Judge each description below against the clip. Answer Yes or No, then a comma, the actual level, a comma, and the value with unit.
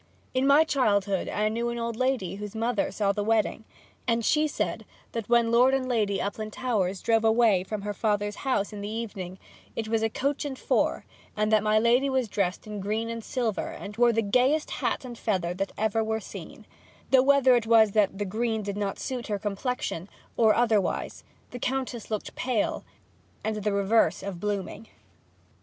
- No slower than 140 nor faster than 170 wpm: No, average, 190 wpm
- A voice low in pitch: No, high, 220 Hz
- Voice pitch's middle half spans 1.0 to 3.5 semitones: Yes, average, 2.8 semitones